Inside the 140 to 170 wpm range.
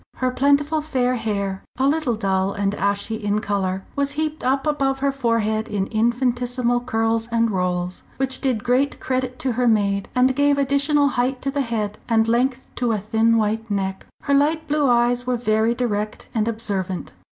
No: average, 180 wpm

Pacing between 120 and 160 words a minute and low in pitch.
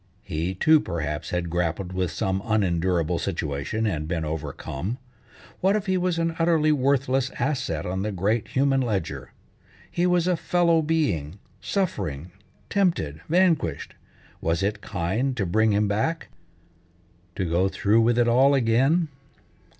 Yes: average, 140 wpm; low, 105 Hz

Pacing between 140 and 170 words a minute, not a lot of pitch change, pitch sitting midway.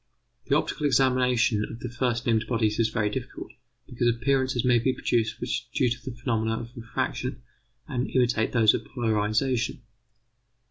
No: average, 165 wpm; narrow, 2.0 semitones; low, 120 Hz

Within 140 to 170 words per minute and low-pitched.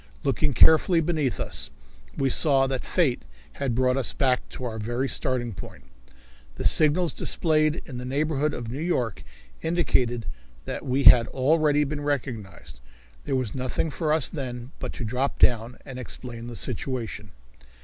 Yes: average, 160 wpm; low, 130 Hz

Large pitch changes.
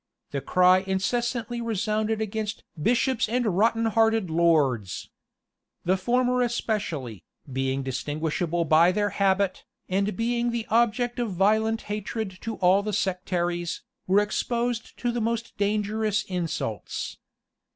No: average, 4.2 semitones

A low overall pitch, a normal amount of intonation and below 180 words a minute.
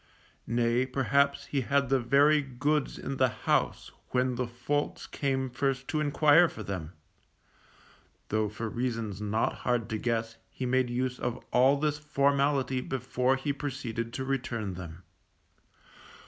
Yes: low, 130 Hz; average, 3.0 semitones; average, 145 wpm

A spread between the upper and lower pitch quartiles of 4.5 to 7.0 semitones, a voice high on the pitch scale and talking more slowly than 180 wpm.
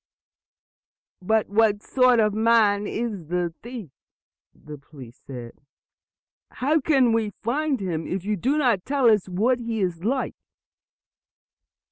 Yes: average, 5.2 semitones; high, 215 Hz; slow, 135 wpm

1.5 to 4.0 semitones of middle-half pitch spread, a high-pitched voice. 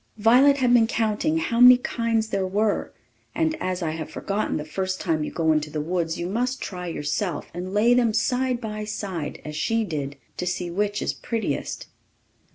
No: average, 5.3 semitones; high, 205 Hz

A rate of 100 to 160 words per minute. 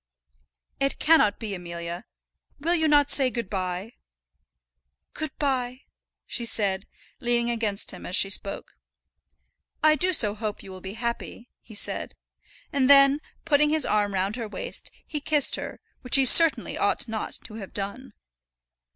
Yes: average, 155 wpm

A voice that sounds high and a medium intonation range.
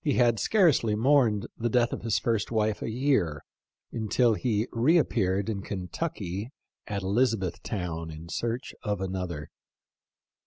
No: low, 110 Hz; average, 4.2 semitones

